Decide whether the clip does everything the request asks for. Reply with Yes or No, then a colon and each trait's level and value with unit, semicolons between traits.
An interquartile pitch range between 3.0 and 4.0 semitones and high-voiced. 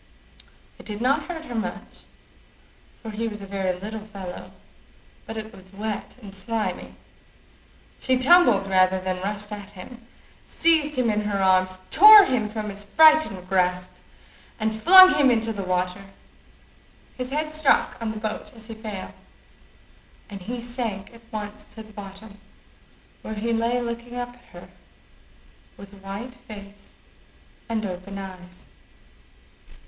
Yes: average, 3.7 semitones; high, 215 Hz